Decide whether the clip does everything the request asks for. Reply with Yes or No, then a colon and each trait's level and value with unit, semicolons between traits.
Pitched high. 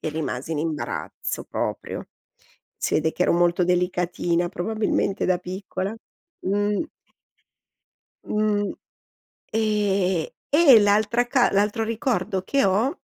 Yes: high, 195 Hz